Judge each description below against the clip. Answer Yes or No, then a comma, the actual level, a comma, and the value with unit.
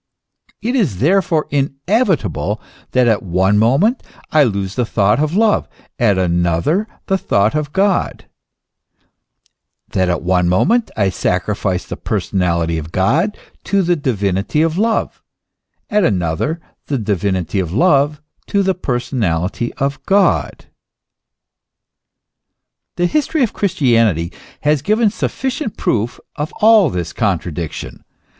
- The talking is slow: Yes, slow, 120 wpm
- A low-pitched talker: Yes, low, 125 Hz